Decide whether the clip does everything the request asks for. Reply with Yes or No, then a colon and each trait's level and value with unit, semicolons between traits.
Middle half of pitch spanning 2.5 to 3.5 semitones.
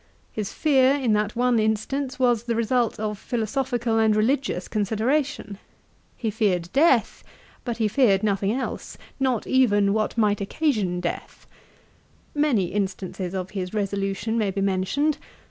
No: average, 4.1 semitones